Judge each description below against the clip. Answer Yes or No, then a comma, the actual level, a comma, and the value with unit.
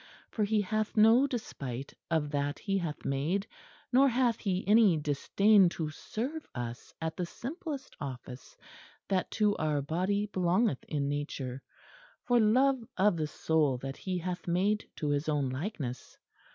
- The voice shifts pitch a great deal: Yes, wide, 6.8 semitones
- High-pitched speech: No, medium, 180 Hz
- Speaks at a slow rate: No, average, 150 wpm